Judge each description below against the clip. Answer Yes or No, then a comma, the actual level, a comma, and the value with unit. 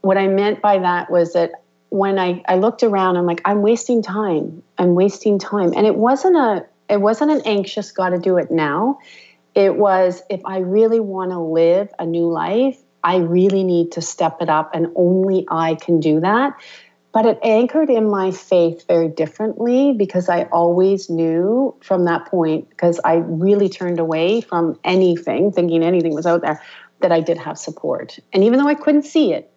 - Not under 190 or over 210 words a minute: Yes, average, 195 wpm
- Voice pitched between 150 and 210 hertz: Yes, medium, 185 Hz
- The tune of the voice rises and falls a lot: No, average, 3.8 semitones